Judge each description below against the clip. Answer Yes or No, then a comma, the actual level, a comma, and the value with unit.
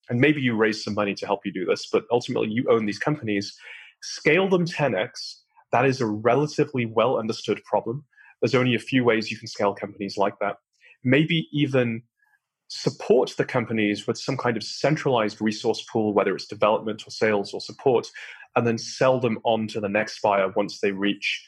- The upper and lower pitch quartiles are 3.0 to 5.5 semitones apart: Yes, average, 3.5 semitones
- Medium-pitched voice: No, low, 115 Hz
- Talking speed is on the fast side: No, average, 195 wpm